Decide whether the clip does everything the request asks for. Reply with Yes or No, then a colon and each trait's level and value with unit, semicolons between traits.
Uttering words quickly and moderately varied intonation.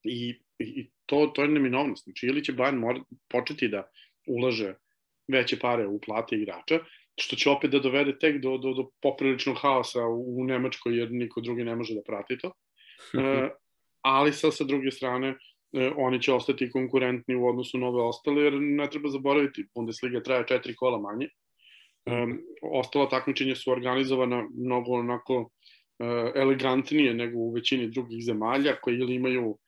No: fast, 165 wpm; narrow, 2.3 semitones